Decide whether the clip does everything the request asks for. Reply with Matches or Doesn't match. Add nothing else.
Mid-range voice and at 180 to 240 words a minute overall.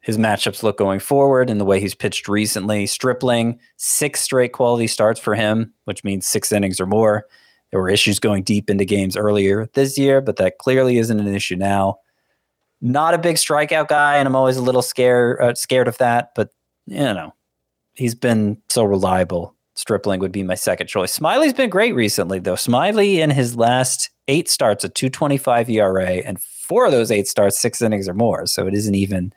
Doesn't match